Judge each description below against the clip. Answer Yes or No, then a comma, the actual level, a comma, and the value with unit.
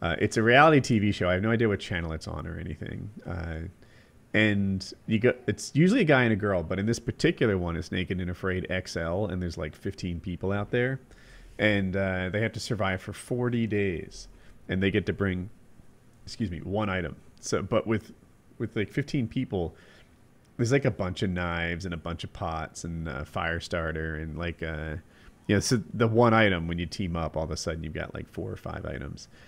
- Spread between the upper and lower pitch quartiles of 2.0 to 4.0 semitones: No, average, 4.8 semitones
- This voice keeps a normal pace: No, fast, 220 wpm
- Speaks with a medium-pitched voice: No, very low, 95 Hz